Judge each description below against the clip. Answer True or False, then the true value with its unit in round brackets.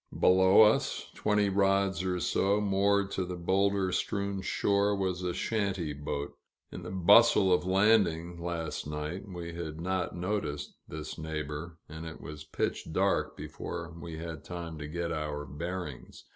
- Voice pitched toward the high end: False (90 Hz)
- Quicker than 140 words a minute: True (155 wpm)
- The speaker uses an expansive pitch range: False (3.4 semitones)